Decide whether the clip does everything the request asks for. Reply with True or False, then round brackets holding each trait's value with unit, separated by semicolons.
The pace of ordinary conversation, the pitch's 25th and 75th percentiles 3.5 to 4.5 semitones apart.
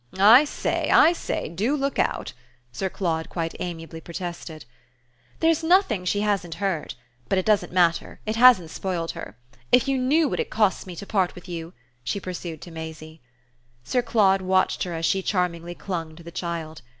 True (180 wpm; 4.2 semitones)